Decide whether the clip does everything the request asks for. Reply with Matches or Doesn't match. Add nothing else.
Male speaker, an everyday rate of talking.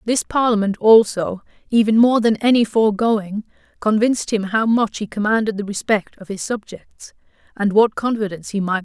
Doesn't match